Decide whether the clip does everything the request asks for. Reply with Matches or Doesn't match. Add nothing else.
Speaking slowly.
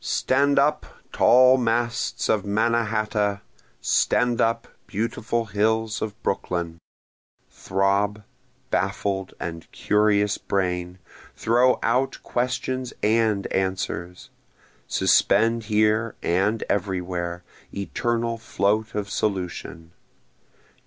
Matches